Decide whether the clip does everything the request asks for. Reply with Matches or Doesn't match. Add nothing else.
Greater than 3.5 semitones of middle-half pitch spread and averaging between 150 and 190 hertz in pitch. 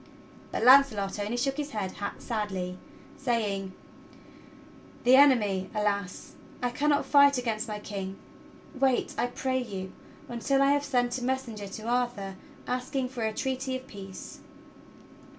Doesn't match